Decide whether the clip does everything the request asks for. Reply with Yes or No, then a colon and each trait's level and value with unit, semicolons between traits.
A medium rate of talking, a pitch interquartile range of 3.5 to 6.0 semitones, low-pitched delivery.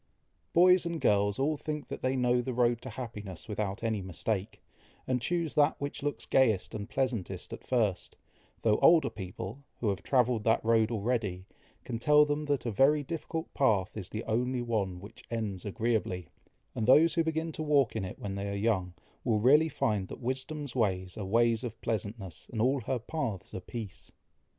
Yes: average, 185 wpm; average, 4.8 semitones; low, 115 Hz